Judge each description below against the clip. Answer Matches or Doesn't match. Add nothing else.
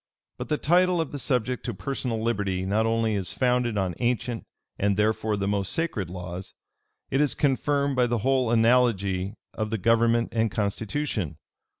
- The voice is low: Matches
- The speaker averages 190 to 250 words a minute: Doesn't match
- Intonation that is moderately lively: Matches